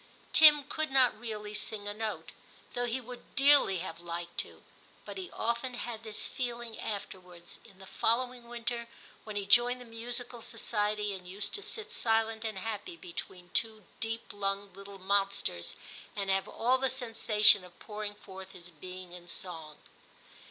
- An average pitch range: Yes, average, 3.8 semitones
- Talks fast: No, average, 175 wpm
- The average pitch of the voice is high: Yes, high, 215 Hz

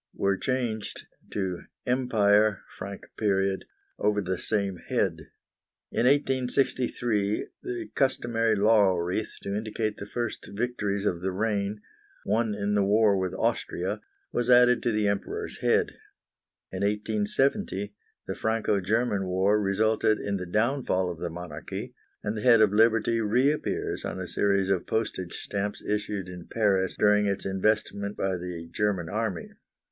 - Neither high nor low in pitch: No, low, 105 Hz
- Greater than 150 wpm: No, average, 140 wpm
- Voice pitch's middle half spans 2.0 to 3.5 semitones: Yes, narrow, 2.6 semitones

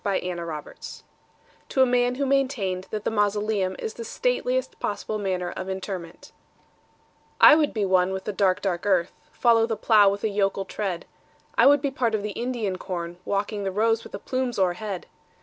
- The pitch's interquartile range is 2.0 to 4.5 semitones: Yes, average, 3.6 semitones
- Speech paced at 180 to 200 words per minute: Yes, average, 190 wpm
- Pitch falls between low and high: No, high, 205 Hz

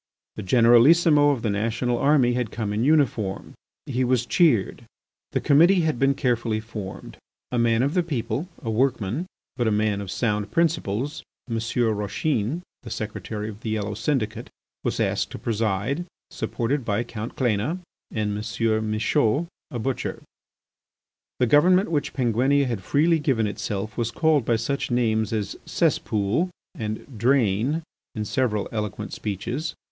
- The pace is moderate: Yes, average, 150 wpm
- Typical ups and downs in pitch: Yes, average, 4.5 semitones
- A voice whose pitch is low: Yes, low, 115 Hz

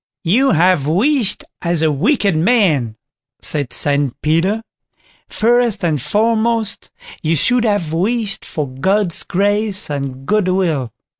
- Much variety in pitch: Yes, wide, 6.3 semitones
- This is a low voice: No, medium, 185 Hz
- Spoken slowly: Yes, slow, 120 wpm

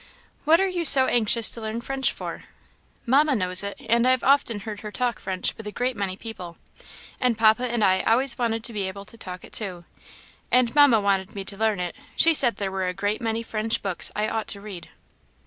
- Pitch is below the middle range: No, high, 220 Hz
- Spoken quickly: Yes, fast, 225 wpm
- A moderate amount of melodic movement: Yes, average, 3.7 semitones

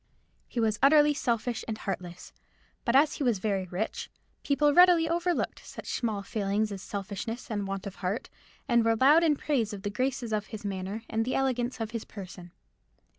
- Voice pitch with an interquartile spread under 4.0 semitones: No, average, 4.9 semitones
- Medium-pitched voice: No, high, 225 Hz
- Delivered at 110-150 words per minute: No, average, 185 wpm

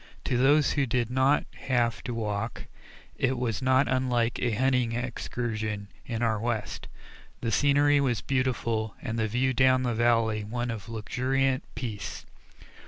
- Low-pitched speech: Yes, low, 120 Hz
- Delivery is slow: No, average, 150 wpm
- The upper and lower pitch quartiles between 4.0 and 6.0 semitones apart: No, narrow, 2.4 semitones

